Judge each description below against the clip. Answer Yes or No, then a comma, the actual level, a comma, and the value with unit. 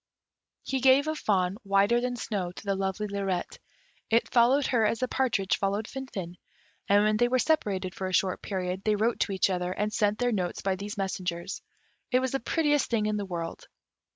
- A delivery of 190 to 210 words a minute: Yes, fast, 205 wpm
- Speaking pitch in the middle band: No, high, 205 Hz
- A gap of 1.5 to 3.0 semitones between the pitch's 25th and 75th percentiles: No, average, 4.1 semitones